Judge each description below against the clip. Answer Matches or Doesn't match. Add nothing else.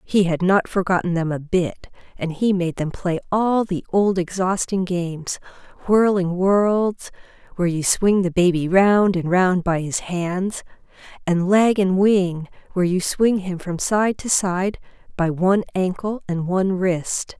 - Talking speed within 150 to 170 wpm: Matches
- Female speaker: Matches